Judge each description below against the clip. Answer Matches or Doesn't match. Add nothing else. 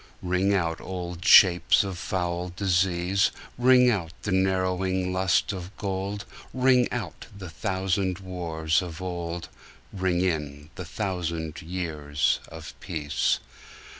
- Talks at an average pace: Doesn't match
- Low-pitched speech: Matches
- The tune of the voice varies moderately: Doesn't match